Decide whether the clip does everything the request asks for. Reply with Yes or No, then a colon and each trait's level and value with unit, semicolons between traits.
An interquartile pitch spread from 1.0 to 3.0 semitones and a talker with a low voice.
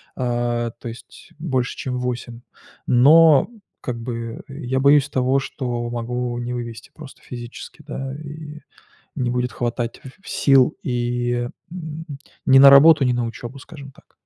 Yes: narrow, 2.4 semitones; low, 125 Hz